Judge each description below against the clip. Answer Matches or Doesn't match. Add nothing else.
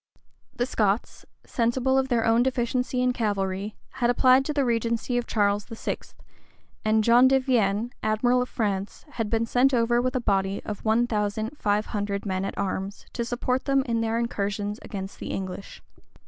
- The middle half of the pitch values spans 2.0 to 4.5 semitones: Matches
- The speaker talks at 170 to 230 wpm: Matches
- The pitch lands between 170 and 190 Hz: Doesn't match